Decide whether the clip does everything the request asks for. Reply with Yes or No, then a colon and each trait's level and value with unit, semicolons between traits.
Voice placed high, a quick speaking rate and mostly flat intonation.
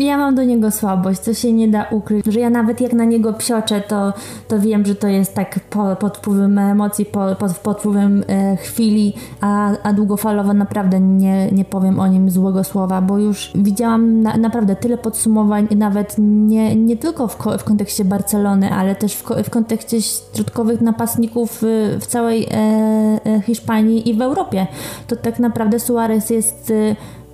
Yes: high, 210 Hz; fast, 180 wpm; narrow, 2.1 semitones